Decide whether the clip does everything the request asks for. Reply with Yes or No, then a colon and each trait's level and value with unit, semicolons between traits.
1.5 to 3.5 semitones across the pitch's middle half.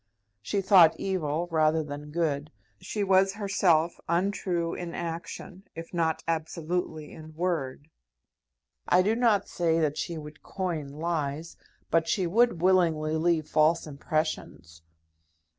Yes: average, 2.8 semitones